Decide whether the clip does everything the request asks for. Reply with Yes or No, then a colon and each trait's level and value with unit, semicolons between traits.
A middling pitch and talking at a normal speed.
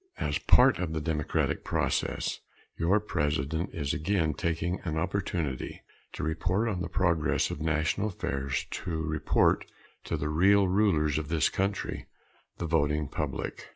No: very low, 80 Hz; average, 145 wpm